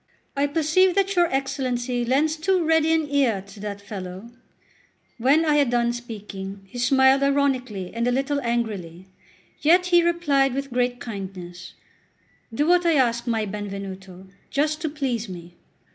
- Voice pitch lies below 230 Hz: No, very high, 250 Hz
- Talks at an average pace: Yes, average, 155 wpm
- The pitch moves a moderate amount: No, wide, 6.3 semitones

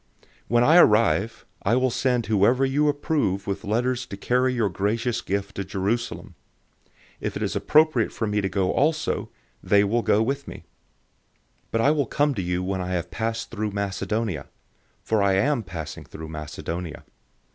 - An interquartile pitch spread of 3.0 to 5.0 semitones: Yes, average, 4.5 semitones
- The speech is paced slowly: No, average, 180 wpm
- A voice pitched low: Yes, low, 110 Hz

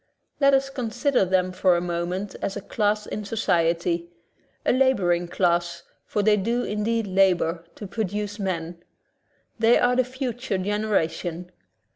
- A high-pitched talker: Yes, high, 200 Hz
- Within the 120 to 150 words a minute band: Yes, average, 140 wpm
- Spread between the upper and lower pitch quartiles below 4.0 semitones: No, average, 4.6 semitones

